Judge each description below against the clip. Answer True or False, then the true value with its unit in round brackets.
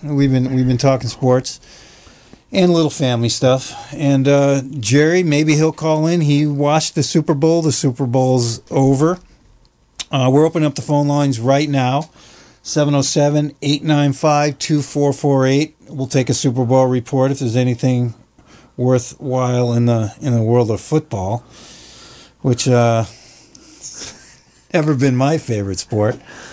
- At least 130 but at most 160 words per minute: True (140 wpm)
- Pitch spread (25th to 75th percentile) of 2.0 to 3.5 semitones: True (2.9 semitones)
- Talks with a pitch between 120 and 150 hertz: True (135 Hz)